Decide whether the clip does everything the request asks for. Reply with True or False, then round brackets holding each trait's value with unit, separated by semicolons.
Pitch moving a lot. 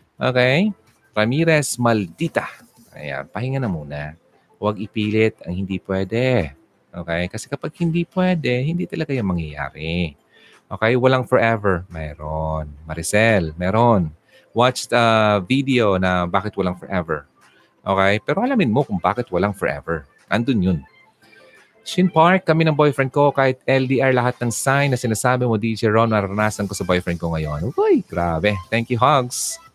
True (6.6 semitones)